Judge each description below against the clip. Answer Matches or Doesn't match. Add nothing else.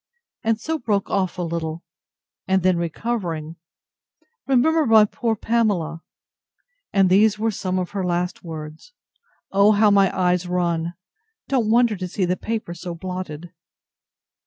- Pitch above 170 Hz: Matches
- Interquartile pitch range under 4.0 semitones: Doesn't match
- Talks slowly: Matches